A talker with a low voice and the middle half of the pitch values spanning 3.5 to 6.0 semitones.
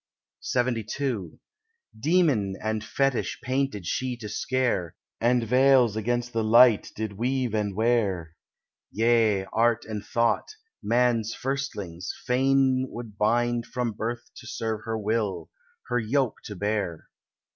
No: low, 115 Hz; average, 2.9 semitones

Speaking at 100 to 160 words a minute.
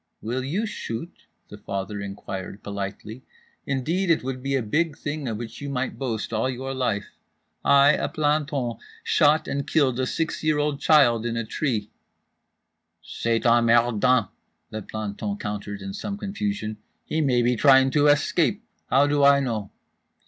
Yes: average, 155 wpm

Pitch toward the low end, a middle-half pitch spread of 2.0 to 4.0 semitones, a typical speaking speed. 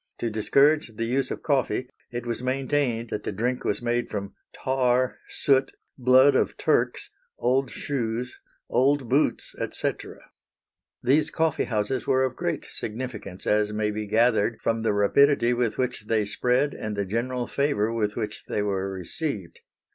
Yes: low, 120 Hz; average, 3.6 semitones; average, 155 wpm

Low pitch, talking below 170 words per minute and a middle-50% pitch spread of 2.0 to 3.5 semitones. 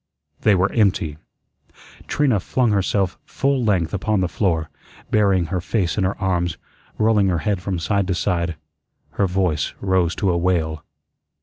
Yes: very low, 95 Hz; average, 160 wpm; average, 2.9 semitones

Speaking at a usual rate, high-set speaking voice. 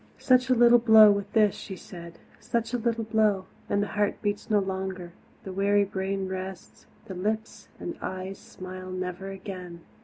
Yes: average, 175 wpm; high, 195 Hz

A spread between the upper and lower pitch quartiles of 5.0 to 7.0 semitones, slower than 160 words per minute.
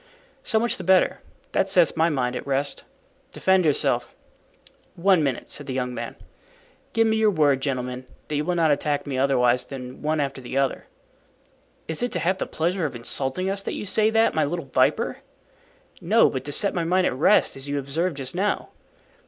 No: wide, 5.5 semitones; average, 200 wpm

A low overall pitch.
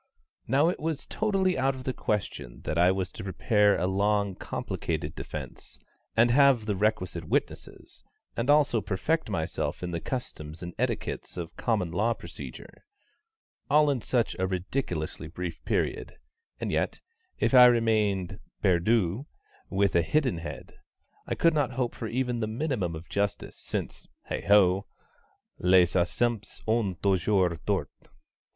Yes: low, 105 Hz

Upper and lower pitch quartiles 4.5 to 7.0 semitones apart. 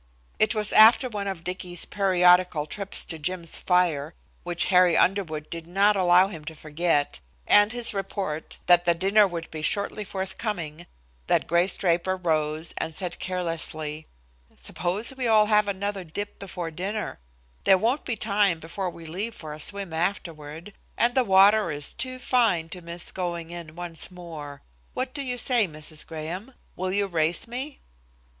No: average, 3.8 semitones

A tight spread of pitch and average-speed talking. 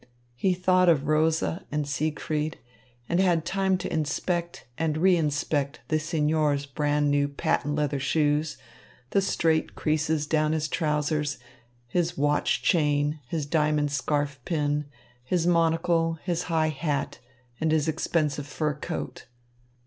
No: narrow, 2.0 semitones; slow, 130 wpm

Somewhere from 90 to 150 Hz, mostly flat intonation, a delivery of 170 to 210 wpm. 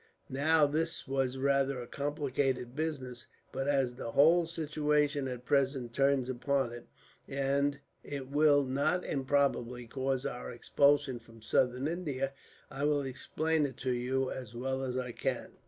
No: low, 135 Hz; narrow, 2.1 semitones; average, 150 wpm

